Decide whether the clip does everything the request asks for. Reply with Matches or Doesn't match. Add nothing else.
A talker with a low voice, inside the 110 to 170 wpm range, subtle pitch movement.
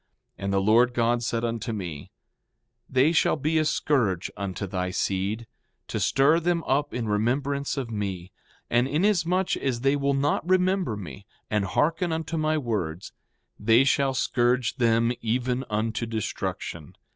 Doesn't match